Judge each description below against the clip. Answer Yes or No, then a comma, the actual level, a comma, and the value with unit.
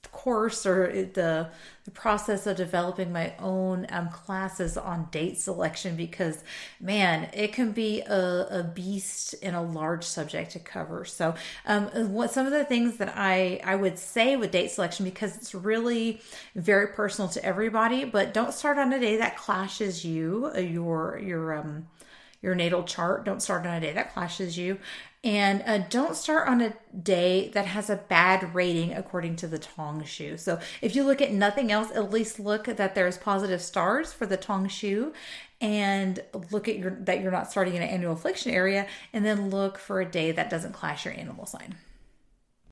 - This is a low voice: No, high, 190 Hz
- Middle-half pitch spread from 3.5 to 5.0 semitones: No, average, 3.1 semitones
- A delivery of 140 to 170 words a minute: No, average, 185 wpm